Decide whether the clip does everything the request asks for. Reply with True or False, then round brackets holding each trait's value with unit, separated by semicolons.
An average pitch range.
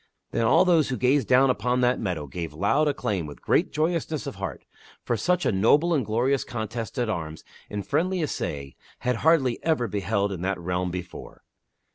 False (7.0 semitones)